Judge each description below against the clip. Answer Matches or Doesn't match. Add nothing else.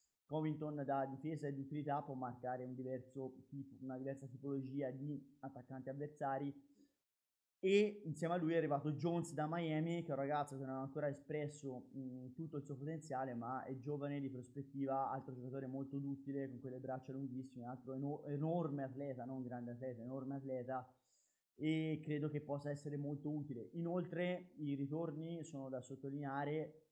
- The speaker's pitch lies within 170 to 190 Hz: Doesn't match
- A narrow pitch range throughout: Matches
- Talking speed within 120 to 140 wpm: Doesn't match